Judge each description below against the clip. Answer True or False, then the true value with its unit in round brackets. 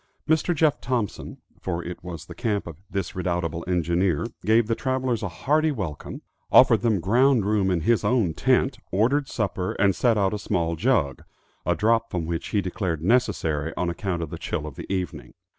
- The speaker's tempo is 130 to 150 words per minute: False (190 wpm)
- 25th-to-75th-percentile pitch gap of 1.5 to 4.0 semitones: False (5.4 semitones)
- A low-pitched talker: True (100 Hz)